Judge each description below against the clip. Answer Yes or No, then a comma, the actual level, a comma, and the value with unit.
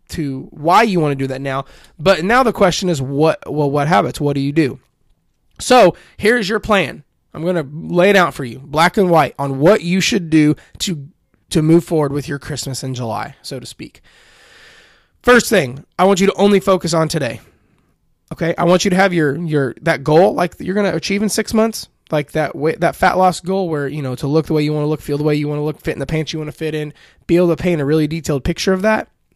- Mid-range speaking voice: Yes, medium, 160 Hz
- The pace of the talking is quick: Yes, fast, 255 wpm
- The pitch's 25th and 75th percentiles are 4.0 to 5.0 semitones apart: Yes, average, 4.3 semitones